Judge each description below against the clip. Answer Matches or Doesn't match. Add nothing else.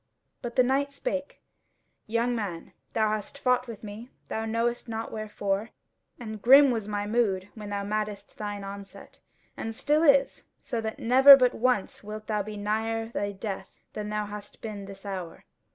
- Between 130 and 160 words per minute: Doesn't match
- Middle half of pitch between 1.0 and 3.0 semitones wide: Matches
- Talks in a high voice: Matches